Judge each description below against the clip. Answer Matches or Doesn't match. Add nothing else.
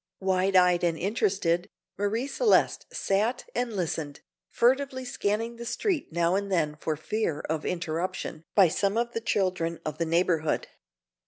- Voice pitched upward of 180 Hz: Matches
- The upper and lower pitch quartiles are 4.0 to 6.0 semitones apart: Matches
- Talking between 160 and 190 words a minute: Doesn't match